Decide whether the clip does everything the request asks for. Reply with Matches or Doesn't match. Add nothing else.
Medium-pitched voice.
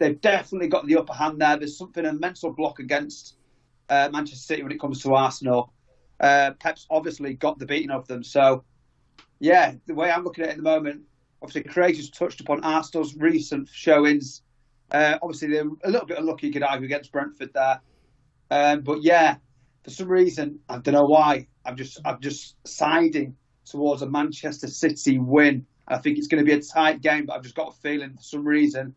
Matches